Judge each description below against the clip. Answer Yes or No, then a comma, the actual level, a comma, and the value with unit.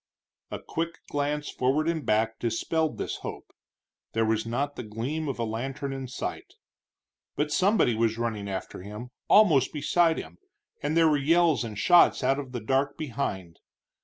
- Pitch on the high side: No, low, 135 Hz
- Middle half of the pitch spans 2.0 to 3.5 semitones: No, wide, 5.4 semitones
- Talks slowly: No, average, 165 wpm